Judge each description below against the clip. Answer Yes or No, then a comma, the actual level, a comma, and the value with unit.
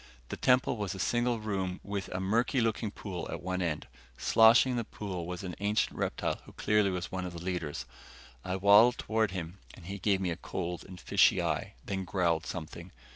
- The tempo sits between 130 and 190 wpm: No, fast, 205 wpm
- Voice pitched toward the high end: No, very low, 95 Hz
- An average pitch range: Yes, average, 3.0 semitones